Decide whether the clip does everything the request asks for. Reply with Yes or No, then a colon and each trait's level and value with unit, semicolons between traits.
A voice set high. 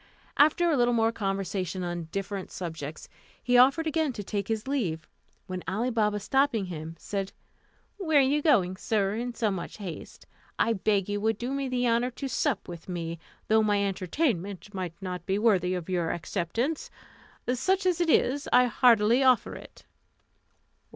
Yes: high, 215 Hz